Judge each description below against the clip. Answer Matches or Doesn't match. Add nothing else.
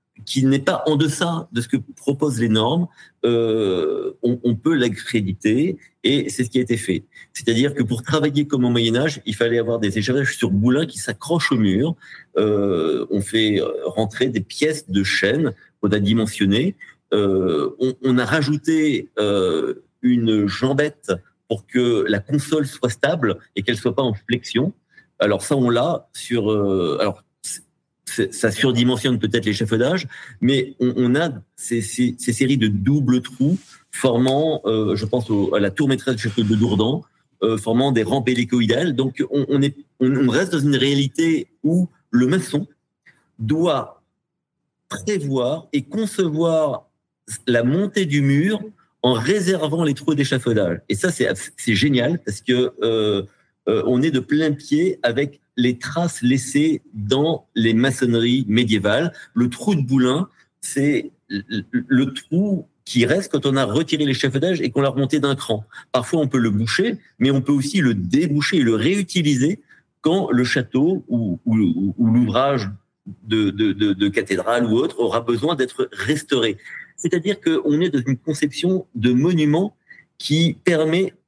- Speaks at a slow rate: Doesn't match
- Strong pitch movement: Doesn't match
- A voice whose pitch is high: Doesn't match